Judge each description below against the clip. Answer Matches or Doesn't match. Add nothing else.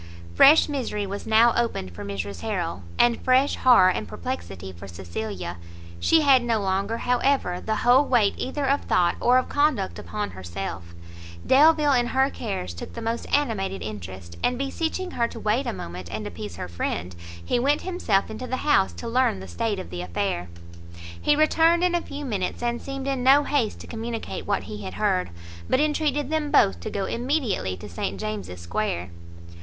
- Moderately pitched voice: Doesn't match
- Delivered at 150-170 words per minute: Doesn't match